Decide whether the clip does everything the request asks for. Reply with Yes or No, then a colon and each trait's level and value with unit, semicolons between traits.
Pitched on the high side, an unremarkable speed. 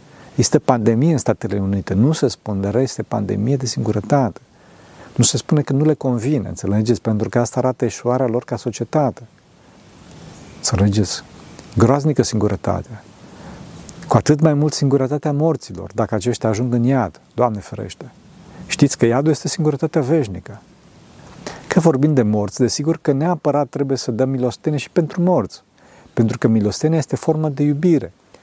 No: low, 125 Hz; average, 150 wpm